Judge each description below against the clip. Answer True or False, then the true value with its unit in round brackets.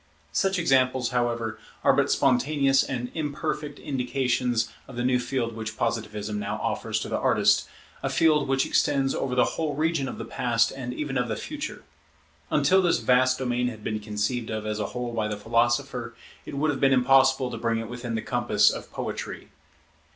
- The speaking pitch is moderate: False (125 Hz)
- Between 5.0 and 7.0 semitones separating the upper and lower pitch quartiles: False (2.8 semitones)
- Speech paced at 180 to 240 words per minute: True (190 wpm)